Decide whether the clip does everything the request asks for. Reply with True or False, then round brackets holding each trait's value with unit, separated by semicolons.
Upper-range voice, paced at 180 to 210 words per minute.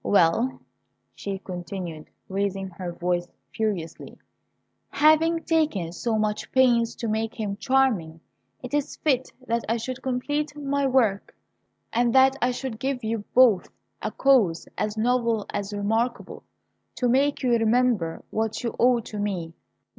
False (230 Hz; 140 wpm)